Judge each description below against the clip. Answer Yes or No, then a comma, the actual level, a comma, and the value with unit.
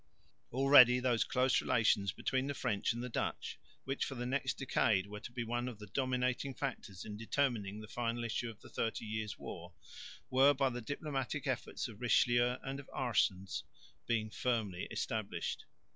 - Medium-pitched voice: No, low, 120 Hz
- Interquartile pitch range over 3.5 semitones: No, average, 3.2 semitones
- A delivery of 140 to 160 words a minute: No, average, 175 wpm